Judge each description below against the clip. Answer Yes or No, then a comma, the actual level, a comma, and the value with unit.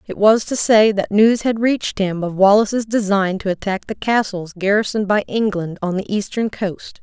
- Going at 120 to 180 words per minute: No, average, 195 wpm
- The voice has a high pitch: Yes, high, 205 Hz